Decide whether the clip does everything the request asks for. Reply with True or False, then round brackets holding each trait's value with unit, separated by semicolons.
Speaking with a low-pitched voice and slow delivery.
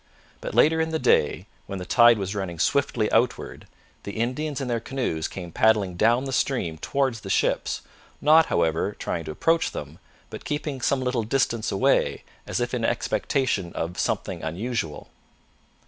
False (115 Hz; 165 wpm)